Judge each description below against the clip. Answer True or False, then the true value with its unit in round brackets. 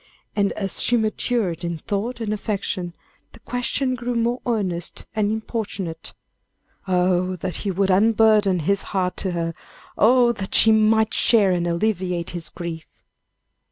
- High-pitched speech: True (200 Hz)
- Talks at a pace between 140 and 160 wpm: True (145 wpm)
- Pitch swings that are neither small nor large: True (3.8 semitones)